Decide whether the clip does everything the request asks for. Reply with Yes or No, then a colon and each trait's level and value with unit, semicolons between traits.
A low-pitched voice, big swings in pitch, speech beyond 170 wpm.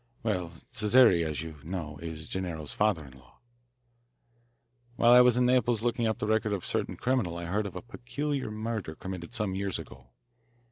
Yes: low, 100 Hz; wide, 5.9 semitones; average, 185 wpm